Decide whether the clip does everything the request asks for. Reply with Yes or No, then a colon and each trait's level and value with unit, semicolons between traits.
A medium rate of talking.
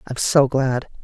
Yes: average, 175 wpm